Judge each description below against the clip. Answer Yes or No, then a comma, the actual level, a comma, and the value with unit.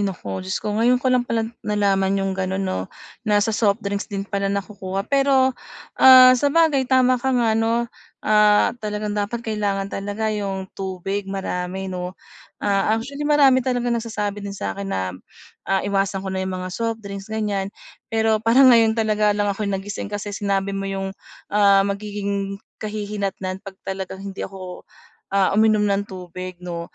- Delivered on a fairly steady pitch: Yes, narrow, 2.3 semitones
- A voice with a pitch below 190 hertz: No, high, 200 Hz